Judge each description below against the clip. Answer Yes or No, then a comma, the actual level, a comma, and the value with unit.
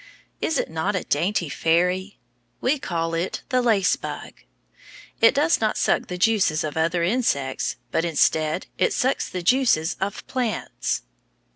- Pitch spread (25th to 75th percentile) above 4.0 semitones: Yes, wide, 5.6 semitones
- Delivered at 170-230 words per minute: No, average, 150 wpm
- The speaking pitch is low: No, medium, 185 Hz